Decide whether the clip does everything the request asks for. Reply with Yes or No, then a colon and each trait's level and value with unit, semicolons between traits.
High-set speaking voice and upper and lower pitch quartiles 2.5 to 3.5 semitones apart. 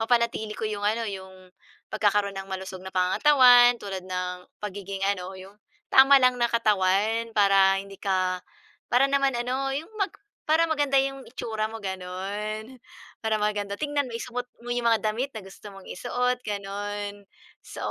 No: high, 215 Hz; average, 4.0 semitones